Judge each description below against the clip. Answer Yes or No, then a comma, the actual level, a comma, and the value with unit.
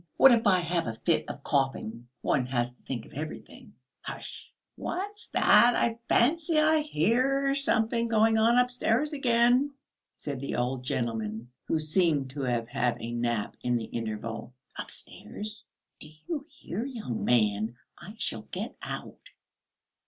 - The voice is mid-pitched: Yes, medium, 170 Hz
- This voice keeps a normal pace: Yes, average, 150 wpm